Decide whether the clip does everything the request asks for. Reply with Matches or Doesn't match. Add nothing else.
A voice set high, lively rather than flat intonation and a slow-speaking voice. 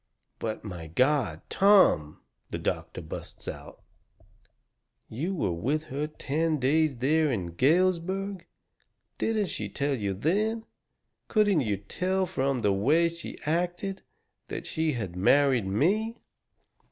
Doesn't match